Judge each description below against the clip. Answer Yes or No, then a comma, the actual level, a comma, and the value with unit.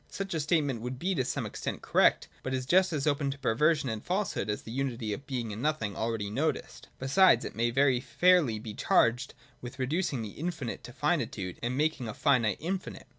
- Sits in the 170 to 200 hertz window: No, low, 130 Hz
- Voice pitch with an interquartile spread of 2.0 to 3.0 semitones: No, average, 5.0 semitones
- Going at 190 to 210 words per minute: Yes, fast, 205 wpm